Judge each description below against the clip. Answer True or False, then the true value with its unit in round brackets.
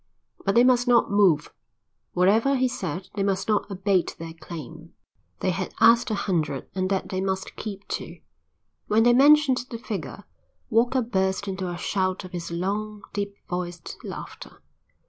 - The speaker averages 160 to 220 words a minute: True (165 wpm)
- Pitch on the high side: True (195 Hz)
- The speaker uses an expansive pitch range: False (3.7 semitones)